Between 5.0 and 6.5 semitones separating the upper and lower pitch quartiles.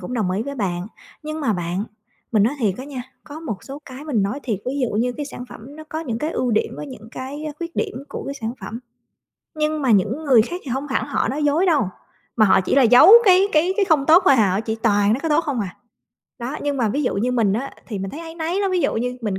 Yes: wide, 5.6 semitones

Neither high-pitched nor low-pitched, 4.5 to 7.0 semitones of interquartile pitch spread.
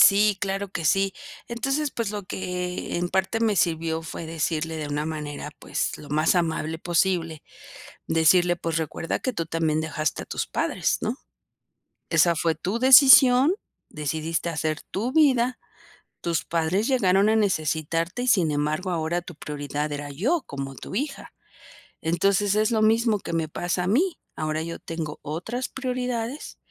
Yes: medium, 175 Hz; average, 5.3 semitones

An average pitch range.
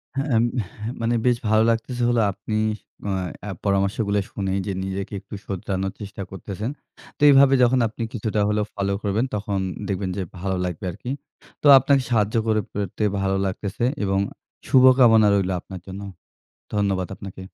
Yes: average, 3.0 semitones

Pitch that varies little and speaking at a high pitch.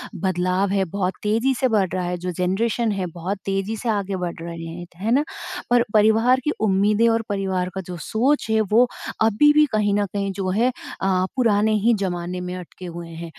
No: average, 3.6 semitones; high, 200 Hz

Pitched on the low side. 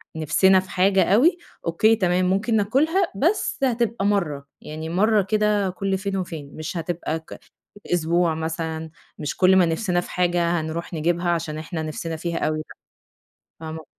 No: medium, 175 Hz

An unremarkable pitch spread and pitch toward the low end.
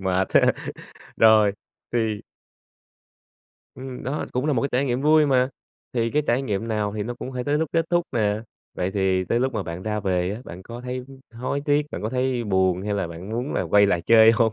Yes: average, 4.3 semitones; low, 115 Hz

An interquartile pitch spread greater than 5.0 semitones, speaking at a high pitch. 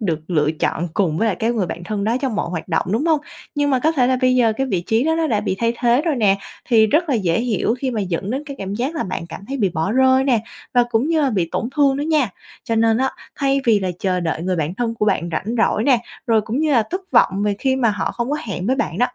Yes: wide, 5.4 semitones; high, 230 Hz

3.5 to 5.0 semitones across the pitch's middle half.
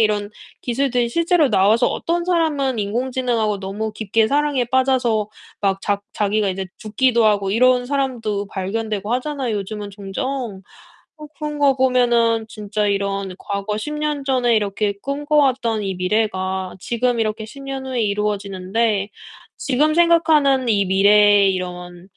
Yes: average, 4.5 semitones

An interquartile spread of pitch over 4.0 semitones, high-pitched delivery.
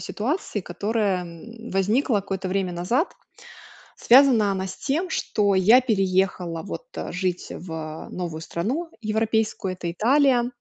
Yes: average, 4.5 semitones; high, 200 Hz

